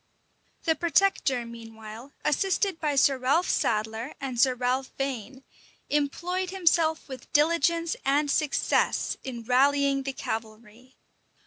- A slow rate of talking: Yes, slow, 115 wpm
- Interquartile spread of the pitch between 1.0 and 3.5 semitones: No, average, 4.5 semitones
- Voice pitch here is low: No, very high, 275 Hz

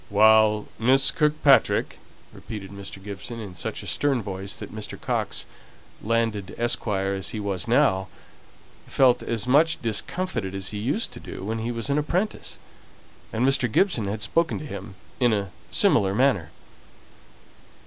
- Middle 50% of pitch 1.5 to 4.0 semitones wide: No, average, 4.8 semitones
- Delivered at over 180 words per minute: No, average, 155 wpm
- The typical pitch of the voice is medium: No, low, 110 Hz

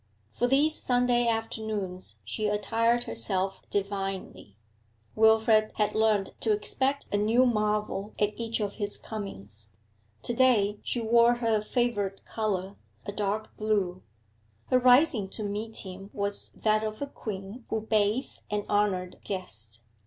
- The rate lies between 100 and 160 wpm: Yes, average, 140 wpm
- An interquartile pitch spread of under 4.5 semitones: Yes, narrow, 2.6 semitones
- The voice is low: No, high, 215 Hz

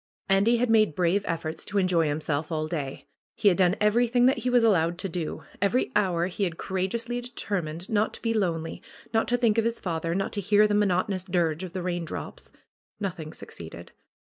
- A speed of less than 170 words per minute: No, average, 200 wpm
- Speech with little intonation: No, average, 4.3 semitones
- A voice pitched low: No, high, 190 Hz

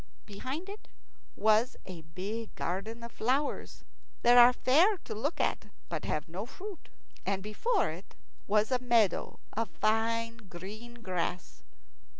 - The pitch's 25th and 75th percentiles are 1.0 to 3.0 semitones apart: No, average, 4.1 semitones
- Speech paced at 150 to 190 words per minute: No, average, 140 wpm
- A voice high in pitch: Yes, high, 225 Hz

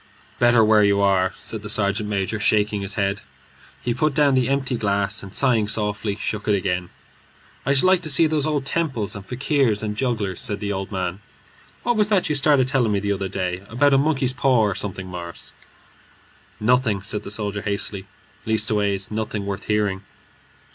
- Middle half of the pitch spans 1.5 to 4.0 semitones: No, average, 4.6 semitones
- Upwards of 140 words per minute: Yes, average, 190 wpm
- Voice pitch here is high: No, low, 105 Hz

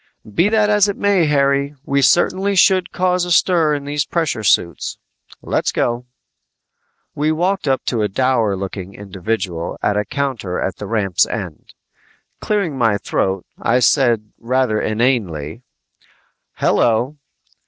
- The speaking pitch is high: No, low, 130 Hz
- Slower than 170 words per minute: Yes, average, 140 wpm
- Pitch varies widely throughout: Yes, wide, 7.7 semitones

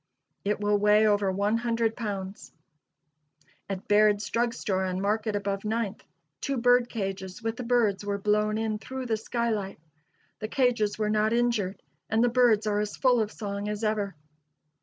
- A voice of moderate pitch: No, high, 215 Hz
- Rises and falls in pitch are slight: Yes, narrow, 2.2 semitones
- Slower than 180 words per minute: Yes, average, 170 wpm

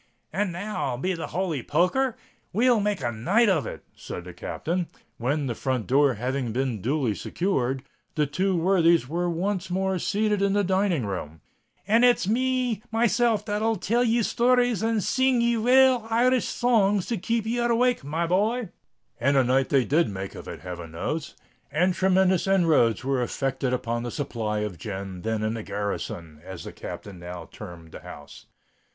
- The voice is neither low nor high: Yes, medium, 170 Hz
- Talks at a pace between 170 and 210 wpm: Yes, average, 175 wpm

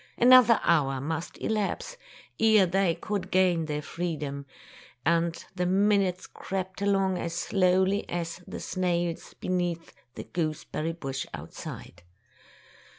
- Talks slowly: Yes, slow, 125 wpm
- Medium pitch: Yes, medium, 180 Hz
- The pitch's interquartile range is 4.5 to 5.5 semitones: No, average, 2.8 semitones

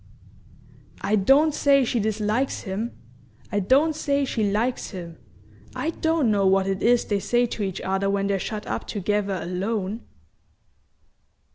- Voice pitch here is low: No, high, 210 Hz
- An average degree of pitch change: Yes, average, 4.2 semitones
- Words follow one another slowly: No, average, 150 wpm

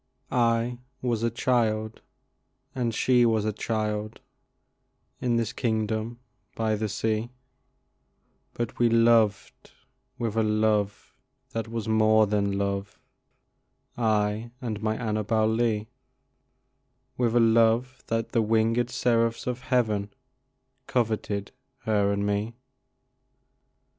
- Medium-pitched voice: No, low, 110 Hz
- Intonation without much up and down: Yes, narrow, 1.6 semitones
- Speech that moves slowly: Yes, slow, 110 wpm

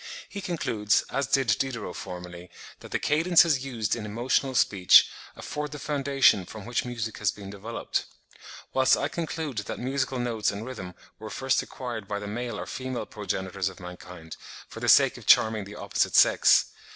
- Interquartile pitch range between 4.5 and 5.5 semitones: Yes, average, 4.8 semitones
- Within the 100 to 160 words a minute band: No, average, 175 wpm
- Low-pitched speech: Yes, low, 115 Hz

